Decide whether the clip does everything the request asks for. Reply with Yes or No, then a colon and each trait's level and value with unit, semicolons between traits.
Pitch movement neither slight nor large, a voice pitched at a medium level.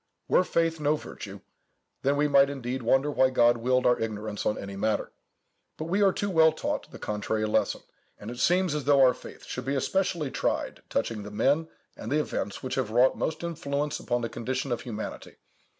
No: average, 4.5 semitones; low, 130 Hz